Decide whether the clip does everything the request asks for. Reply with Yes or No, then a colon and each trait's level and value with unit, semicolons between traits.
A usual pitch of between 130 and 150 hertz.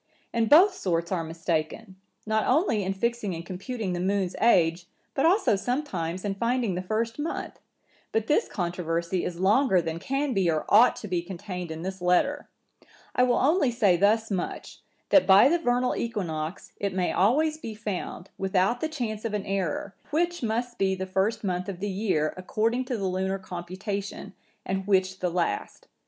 No: high, 195 Hz